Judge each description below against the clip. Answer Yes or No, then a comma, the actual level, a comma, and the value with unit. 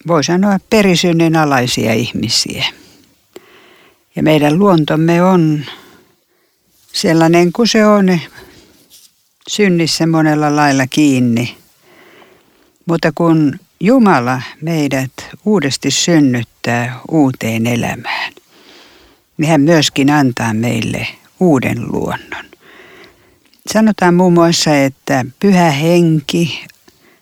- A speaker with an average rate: No, slow, 85 wpm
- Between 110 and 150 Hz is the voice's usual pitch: No, medium, 160 Hz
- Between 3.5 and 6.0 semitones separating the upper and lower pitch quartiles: Yes, average, 4.6 semitones